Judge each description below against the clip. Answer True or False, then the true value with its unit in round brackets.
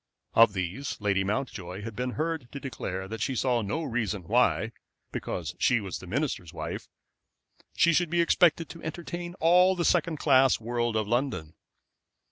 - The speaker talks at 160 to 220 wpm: True (165 wpm)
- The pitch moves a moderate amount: False (7.4 semitones)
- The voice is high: False (125 Hz)